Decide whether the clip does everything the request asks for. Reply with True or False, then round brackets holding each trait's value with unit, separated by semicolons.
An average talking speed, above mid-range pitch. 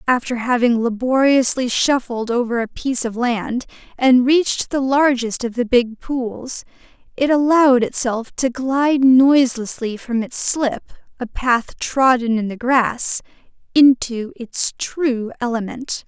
False (125 wpm; 250 Hz)